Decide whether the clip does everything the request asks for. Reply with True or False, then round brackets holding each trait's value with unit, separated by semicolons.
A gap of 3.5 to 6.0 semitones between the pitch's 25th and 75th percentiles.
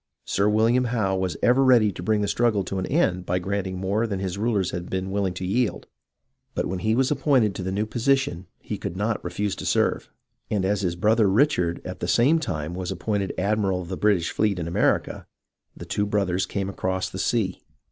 False (3.0 semitones)